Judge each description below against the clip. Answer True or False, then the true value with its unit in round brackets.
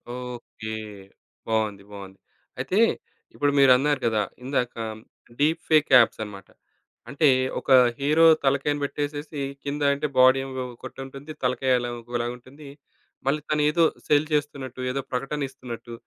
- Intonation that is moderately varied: True (3.2 semitones)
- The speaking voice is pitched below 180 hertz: True (135 Hz)